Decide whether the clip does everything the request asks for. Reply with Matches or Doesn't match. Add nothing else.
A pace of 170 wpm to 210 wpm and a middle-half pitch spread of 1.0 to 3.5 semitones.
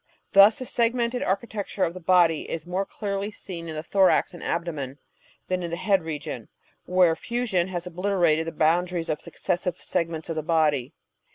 Matches